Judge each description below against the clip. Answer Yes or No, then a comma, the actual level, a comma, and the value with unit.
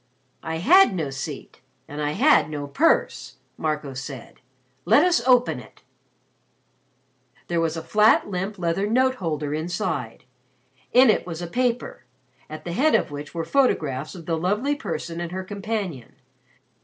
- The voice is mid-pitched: Yes, medium, 175 Hz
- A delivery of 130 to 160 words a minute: Yes, average, 155 wpm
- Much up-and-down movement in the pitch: Yes, wide, 6.2 semitones